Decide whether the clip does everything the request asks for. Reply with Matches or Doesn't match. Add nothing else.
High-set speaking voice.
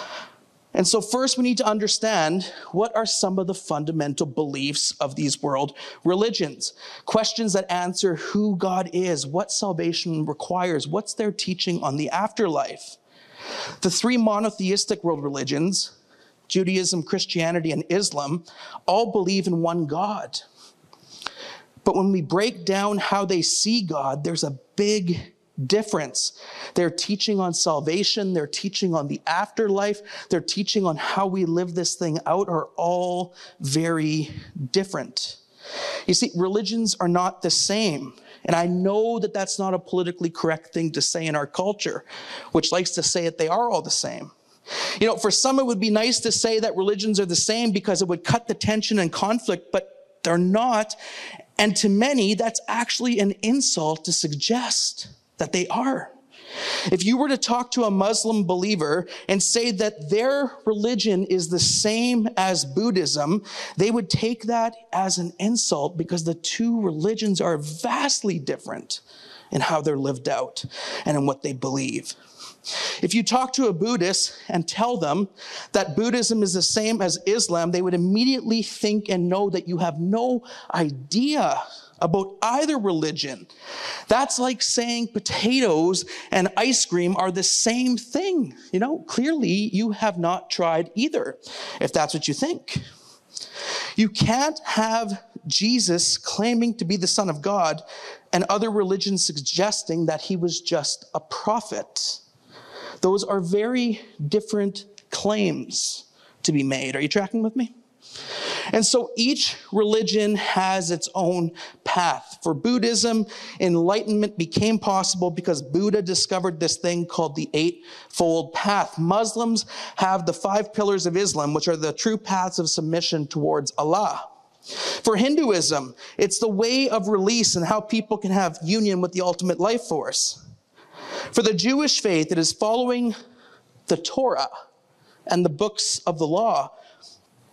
Matches